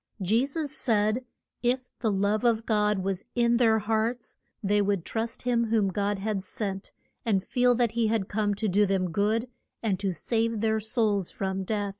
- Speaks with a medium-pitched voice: No, high, 215 Hz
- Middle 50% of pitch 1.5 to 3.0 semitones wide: Yes, narrow, 2.5 semitones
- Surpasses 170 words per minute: Yes, average, 185 wpm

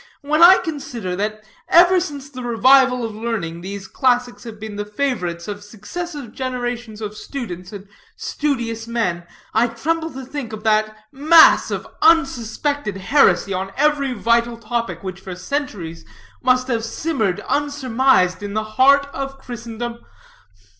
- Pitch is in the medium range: No, high, 235 Hz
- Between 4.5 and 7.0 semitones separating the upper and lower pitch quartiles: Yes, average, 4.8 semitones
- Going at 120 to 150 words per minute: Yes, average, 145 wpm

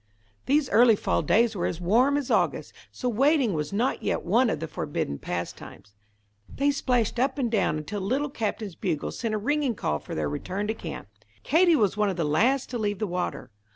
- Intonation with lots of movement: Yes, wide, 6.4 semitones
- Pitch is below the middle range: No, high, 220 Hz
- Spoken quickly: Yes, fast, 210 wpm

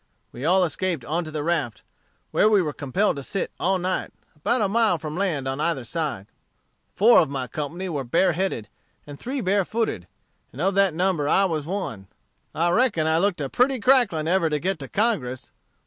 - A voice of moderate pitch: Yes, medium, 170 Hz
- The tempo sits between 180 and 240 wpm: Yes, average, 195 wpm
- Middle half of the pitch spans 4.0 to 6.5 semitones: Yes, average, 5.1 semitones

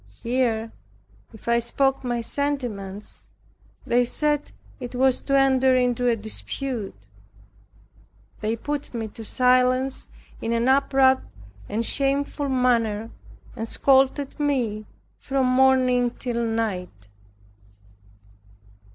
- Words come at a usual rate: No, slow, 105 wpm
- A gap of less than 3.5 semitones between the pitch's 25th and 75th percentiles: Yes, average, 2.8 semitones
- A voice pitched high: Yes, very high, 250 Hz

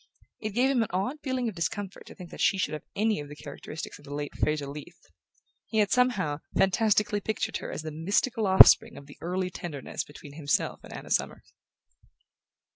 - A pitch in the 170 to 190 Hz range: Yes, medium, 185 Hz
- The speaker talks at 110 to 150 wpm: No, average, 200 wpm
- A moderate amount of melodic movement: No, wide, 6.2 semitones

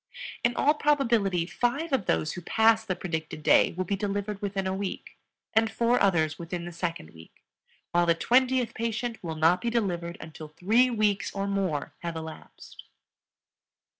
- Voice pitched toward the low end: No, high, 195 Hz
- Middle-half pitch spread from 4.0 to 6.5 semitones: Yes, average, 5.2 semitones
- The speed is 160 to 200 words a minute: Yes, average, 165 wpm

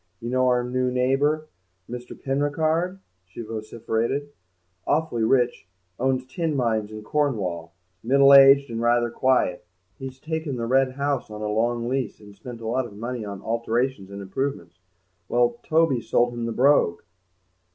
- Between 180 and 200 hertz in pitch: No, low, 125 Hz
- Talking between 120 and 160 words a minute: Yes, average, 155 wpm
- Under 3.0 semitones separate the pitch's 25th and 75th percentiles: No, average, 3.3 semitones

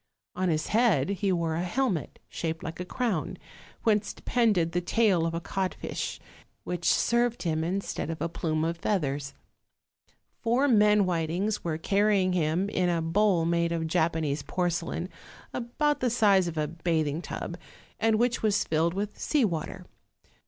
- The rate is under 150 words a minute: No, average, 160 wpm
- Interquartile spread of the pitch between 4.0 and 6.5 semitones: Yes, average, 4.4 semitones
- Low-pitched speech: No, medium, 175 Hz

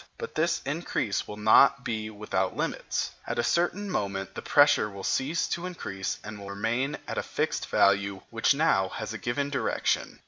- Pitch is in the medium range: No, low, 110 Hz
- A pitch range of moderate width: No, wide, 6.4 semitones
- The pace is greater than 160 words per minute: Yes, average, 180 wpm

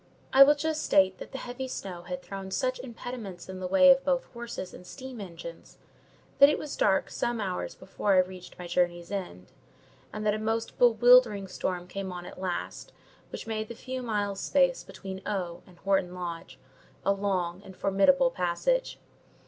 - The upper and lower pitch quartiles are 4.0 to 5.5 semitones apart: Yes, average, 5.2 semitones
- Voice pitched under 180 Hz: No, high, 195 Hz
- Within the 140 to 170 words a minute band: No, average, 180 wpm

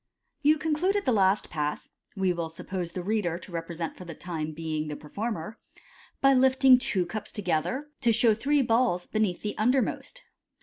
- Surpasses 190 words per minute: No, average, 180 wpm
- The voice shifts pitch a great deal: Yes, wide, 7.0 semitones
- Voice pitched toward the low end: No, high, 205 Hz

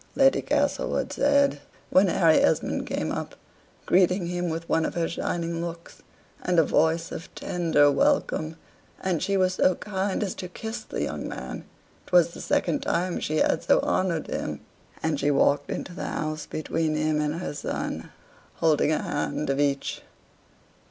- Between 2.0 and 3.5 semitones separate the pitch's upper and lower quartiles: Yes, average, 3.1 semitones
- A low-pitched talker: No, medium, 170 Hz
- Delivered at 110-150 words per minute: No, average, 165 wpm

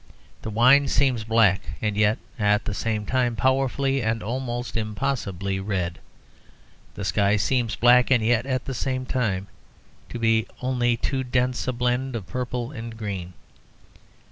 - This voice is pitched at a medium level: No, low, 115 Hz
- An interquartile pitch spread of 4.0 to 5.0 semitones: No, average, 3.3 semitones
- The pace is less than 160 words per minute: Yes, average, 150 wpm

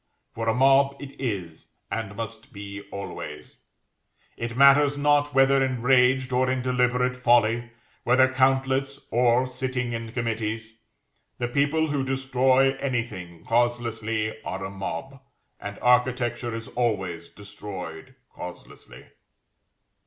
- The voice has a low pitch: Yes, low, 125 Hz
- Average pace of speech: No, slow, 115 wpm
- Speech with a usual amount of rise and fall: Yes, average, 3.0 semitones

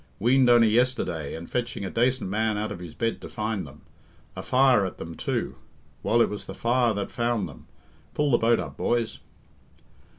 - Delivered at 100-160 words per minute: No, average, 195 wpm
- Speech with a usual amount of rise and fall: Yes, average, 3.3 semitones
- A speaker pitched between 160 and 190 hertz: No, low, 115 Hz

